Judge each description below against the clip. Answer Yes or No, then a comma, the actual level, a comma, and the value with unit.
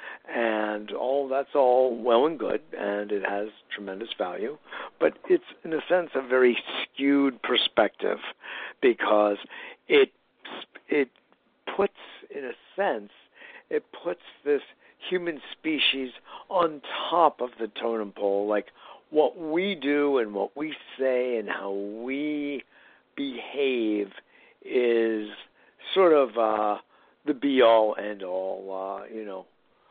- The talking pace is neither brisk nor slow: No, slow, 125 wpm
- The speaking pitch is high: No, low, 130 Hz